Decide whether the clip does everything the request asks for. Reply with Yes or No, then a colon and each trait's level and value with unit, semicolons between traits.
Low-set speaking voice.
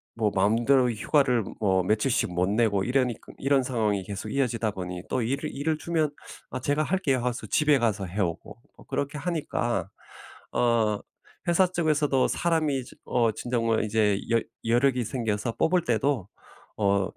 Yes: low, 120 Hz